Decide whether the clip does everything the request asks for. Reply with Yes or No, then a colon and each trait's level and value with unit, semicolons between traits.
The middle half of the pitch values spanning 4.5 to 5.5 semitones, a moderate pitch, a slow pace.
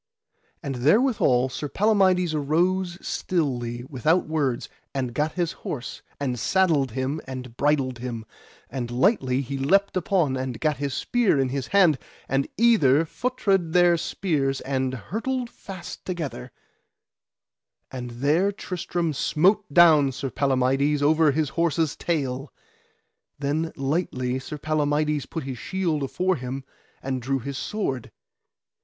Yes: average, 4.9 semitones; medium, 145 Hz; slow, 130 wpm